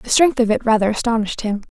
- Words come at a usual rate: No, fast, 245 wpm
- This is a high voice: Yes, high, 225 Hz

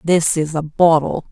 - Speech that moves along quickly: No, average, 180 wpm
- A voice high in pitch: No, medium, 160 Hz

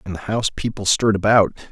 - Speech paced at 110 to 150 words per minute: No, fast, 210 wpm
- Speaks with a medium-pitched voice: No, low, 105 Hz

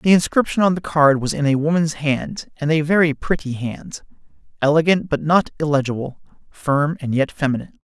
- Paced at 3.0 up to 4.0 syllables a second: No, 5.4 syllables/s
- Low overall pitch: No, medium, 150 Hz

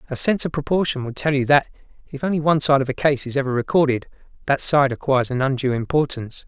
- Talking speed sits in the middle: No, fast, 225 wpm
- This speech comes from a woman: No, male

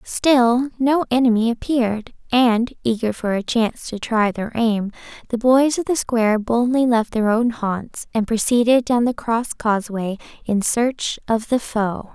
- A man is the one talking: No, female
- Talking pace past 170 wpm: No, average, 165 wpm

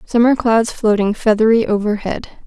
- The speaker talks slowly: Yes, slow, 120 wpm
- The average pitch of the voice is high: Yes, high, 220 Hz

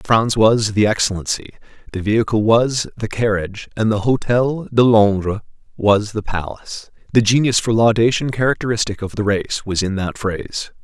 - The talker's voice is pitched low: Yes, low, 110 Hz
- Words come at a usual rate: Yes, average, 160 wpm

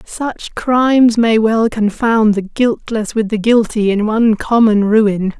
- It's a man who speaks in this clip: No, female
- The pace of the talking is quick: No, average, 155 wpm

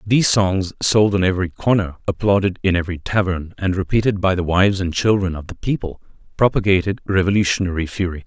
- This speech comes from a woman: No, male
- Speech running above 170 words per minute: No, average, 165 wpm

